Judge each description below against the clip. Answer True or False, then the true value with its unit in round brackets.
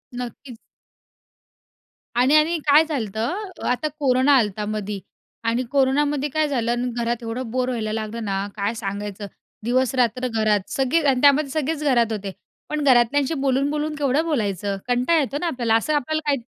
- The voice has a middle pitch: False (250 Hz)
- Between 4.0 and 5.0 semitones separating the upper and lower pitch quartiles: True (4.4 semitones)